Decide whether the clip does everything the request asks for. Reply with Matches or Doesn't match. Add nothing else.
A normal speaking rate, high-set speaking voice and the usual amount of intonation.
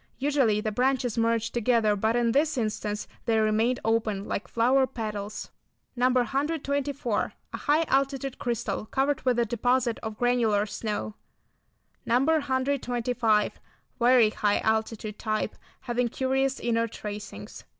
Doesn't match